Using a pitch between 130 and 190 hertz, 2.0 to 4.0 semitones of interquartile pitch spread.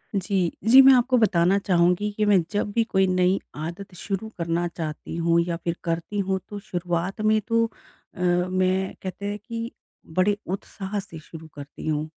Yes: medium, 185 Hz; average, 3.3 semitones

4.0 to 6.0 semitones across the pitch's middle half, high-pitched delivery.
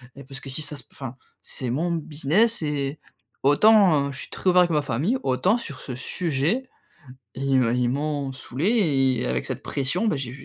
No: average, 4.3 semitones; medium, 140 Hz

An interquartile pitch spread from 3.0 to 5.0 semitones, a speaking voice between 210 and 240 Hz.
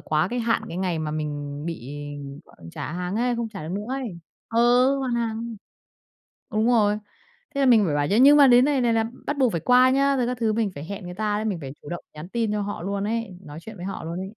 No: wide, 5.5 semitones; high, 215 Hz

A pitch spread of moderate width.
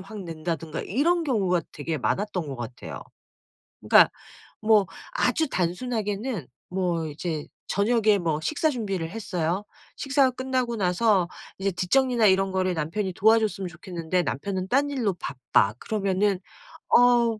Yes: average, 4.9 semitones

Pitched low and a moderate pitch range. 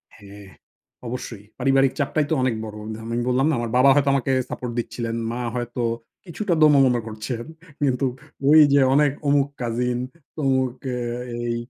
Yes: low, 125 Hz; average, 3.0 semitones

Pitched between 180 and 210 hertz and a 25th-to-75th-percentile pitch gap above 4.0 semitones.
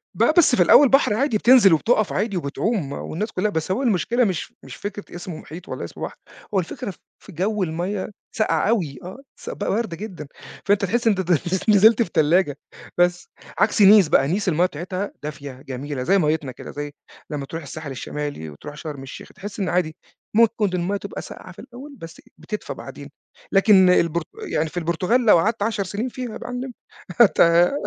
Yes: medium, 185 Hz; average, 5.2 semitones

